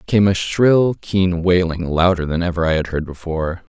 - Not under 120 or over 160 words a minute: No, average, 175 wpm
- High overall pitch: No, very low, 90 Hz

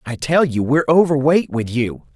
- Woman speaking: No, male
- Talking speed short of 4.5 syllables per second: No, 5.2 syllables/s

